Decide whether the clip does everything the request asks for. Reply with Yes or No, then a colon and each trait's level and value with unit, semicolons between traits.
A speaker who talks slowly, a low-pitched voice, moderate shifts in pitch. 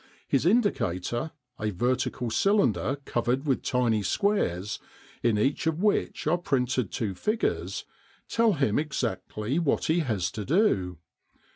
No: slow, 130 wpm; low, 130 Hz; wide, 7.2 semitones